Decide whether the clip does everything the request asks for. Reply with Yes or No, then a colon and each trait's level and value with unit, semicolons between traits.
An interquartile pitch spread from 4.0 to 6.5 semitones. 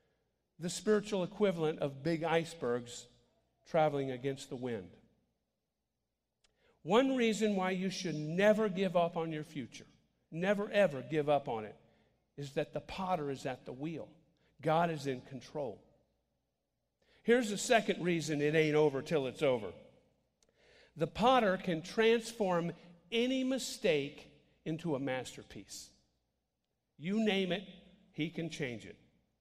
Yes: average, 5.1 semitones